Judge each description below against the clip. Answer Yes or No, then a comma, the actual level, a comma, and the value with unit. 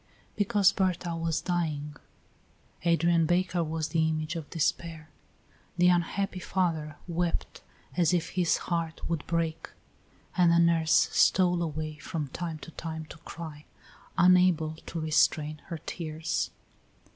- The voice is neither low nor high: Yes, medium, 165 Hz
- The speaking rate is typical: No, slow, 130 wpm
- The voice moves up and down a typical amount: No, narrow, 1.8 semitones